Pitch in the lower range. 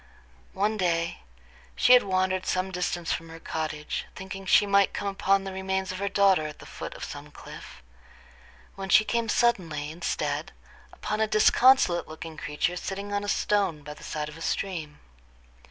No: high, 190 Hz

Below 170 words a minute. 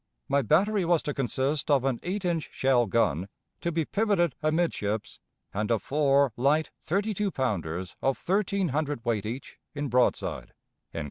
Yes: average, 155 wpm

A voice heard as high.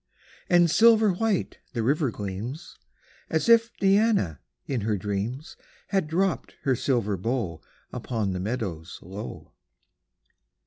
No: low, 125 Hz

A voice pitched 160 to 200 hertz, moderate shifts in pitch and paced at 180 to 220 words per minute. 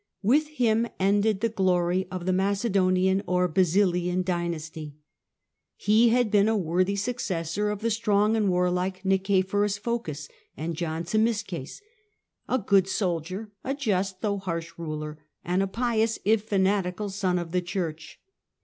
No: high, 190 Hz; average, 3.0 semitones; average, 140 wpm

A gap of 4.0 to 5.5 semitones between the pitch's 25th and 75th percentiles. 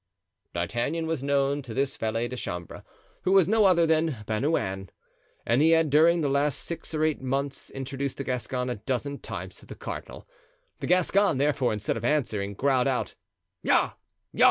Yes: average, 4.3 semitones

